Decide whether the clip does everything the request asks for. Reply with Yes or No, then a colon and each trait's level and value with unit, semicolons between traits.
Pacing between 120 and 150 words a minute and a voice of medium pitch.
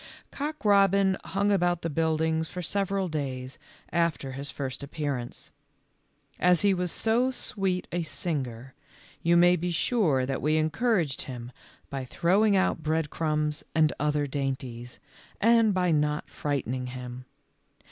Yes: slow, 135 wpm; medium, 160 Hz